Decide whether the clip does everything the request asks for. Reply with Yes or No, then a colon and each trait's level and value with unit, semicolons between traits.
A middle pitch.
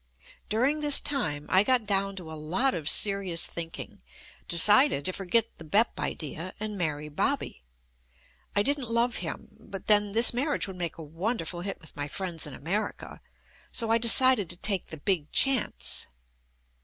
No: high, 195 Hz